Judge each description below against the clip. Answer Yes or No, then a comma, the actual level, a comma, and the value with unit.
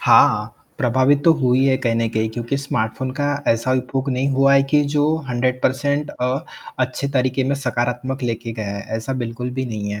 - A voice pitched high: No, low, 130 Hz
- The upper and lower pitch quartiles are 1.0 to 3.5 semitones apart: Yes, average, 2.7 semitones